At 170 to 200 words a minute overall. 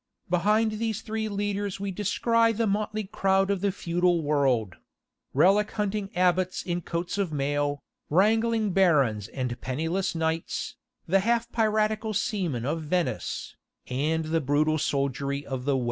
No: average, 145 wpm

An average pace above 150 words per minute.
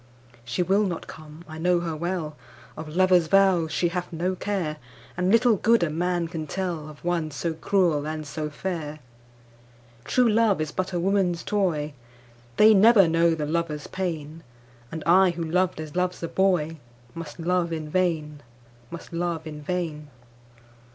No: average, 145 wpm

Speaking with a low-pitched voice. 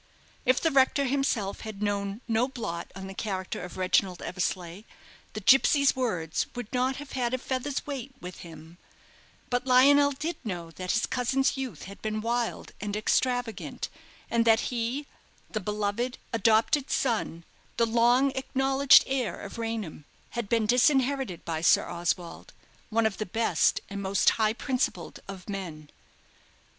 No: high, 230 Hz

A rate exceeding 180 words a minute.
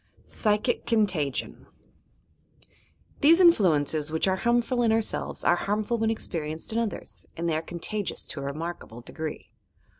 No: average, 145 wpm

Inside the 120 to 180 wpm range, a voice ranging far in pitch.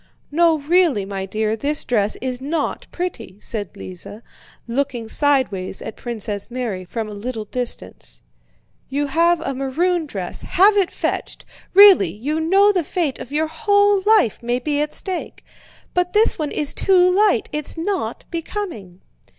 Yes: average, 155 wpm; wide, 8.0 semitones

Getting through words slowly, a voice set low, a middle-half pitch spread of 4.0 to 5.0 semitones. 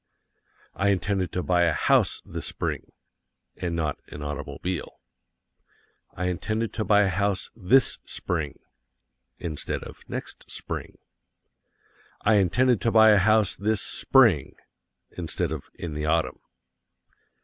Yes: slow, 125 wpm; very low, 95 Hz; average, 4.5 semitones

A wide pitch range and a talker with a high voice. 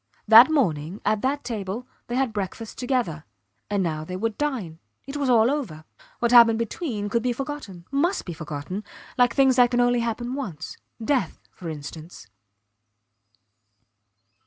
Yes: wide, 5.8 semitones; high, 230 Hz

